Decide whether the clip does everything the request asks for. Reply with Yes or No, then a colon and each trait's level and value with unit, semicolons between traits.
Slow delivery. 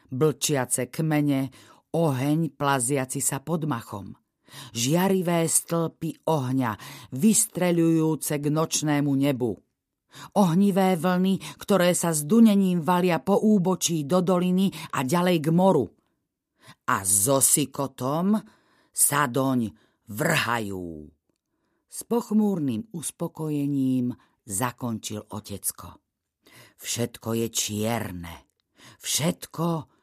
Yes: slow, 90 wpm